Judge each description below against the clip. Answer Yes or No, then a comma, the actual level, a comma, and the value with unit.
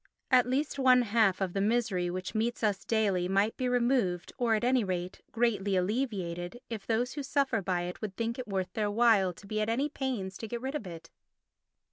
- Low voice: No, high, 220 Hz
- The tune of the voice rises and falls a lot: No, average, 4.3 semitones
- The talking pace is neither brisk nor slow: No, fast, 210 wpm